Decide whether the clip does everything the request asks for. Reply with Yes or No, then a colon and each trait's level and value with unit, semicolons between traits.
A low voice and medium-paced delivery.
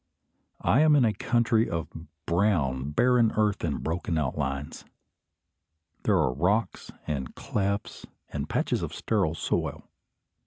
No: very low, 90 Hz; slow, 125 wpm